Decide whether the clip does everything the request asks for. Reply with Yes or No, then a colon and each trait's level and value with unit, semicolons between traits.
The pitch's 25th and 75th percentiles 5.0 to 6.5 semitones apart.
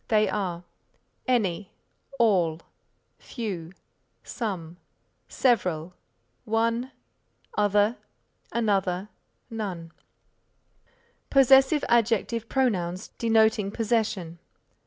No: average, 4.3 semitones